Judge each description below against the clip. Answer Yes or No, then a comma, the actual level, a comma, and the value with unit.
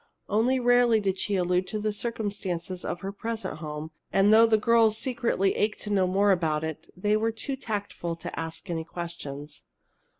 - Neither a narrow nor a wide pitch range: Yes, average, 4.4 semitones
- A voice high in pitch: Yes, high, 200 Hz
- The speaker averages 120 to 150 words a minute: No, average, 180 wpm